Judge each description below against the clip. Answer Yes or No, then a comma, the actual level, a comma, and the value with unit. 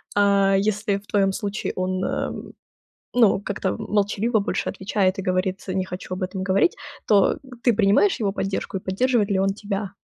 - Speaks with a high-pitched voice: Yes, high, 195 Hz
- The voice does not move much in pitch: Yes, narrow, 1.6 semitones